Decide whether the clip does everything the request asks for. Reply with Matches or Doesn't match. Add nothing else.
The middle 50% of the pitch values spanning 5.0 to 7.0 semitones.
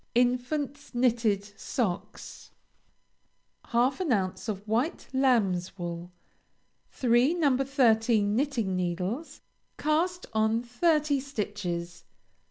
Matches